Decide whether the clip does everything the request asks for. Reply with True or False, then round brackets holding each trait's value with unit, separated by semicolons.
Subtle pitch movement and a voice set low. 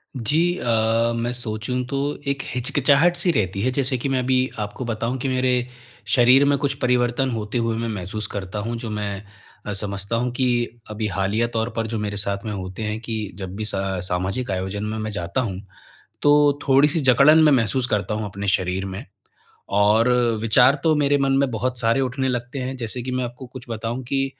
False (3.7 semitones; 120 Hz)